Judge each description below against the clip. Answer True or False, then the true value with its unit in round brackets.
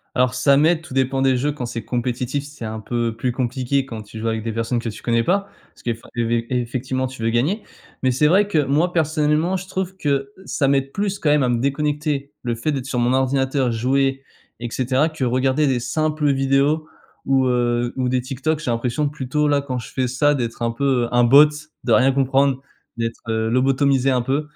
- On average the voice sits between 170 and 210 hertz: False (130 Hz)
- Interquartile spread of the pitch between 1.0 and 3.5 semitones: True (3.2 semitones)